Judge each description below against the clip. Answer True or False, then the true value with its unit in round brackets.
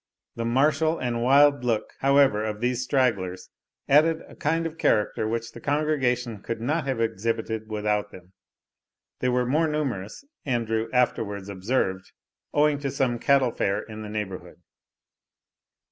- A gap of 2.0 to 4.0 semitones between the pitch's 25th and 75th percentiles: False (4.6 semitones)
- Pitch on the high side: False (120 Hz)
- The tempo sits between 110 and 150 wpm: True (145 wpm)